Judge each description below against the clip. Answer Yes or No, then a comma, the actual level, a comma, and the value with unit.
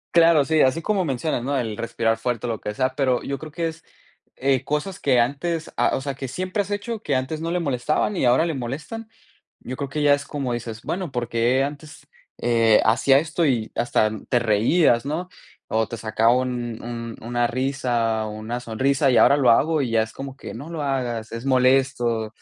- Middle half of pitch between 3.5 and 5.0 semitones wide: Yes, average, 4.1 semitones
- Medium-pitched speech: No, low, 130 Hz